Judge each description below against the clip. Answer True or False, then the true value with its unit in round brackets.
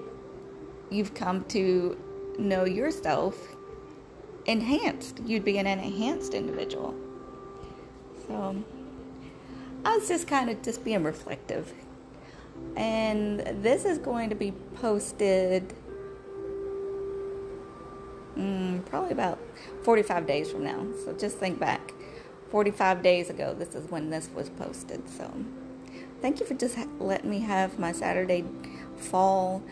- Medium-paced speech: False (120 wpm)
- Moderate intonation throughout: False (6.6 semitones)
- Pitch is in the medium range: False (210 Hz)